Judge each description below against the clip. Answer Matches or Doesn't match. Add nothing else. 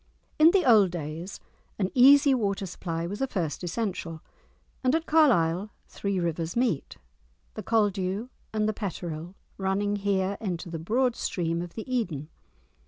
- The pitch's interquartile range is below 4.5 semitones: Doesn't match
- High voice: Matches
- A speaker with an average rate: Matches